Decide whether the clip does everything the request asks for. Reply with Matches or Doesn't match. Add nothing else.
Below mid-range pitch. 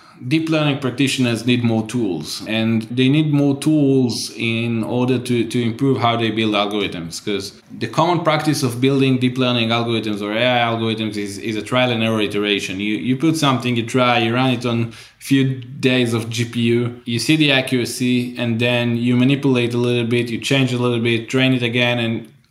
Matches